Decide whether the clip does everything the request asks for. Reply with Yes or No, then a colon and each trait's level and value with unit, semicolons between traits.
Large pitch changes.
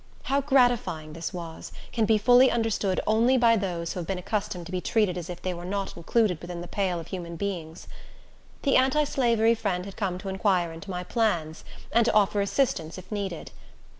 No: average, 4.4 semitones